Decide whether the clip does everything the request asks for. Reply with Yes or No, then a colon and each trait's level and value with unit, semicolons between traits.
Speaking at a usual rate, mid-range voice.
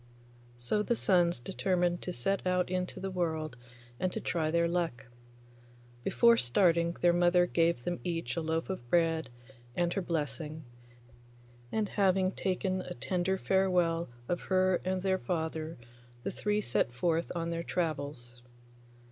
Yes: average, 145 wpm; medium, 175 Hz